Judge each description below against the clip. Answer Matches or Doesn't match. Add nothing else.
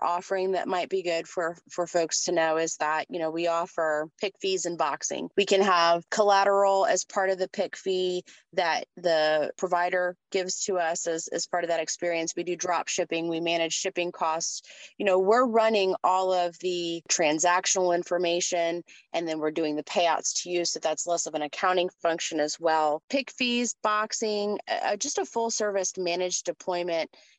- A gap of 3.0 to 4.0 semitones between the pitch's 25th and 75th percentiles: Doesn't match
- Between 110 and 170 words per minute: Doesn't match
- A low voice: Doesn't match